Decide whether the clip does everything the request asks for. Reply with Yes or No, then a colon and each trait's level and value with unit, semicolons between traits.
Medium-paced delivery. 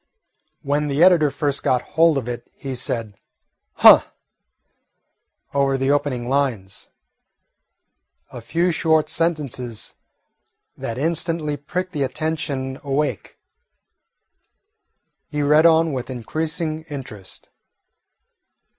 No: slow, 100 wpm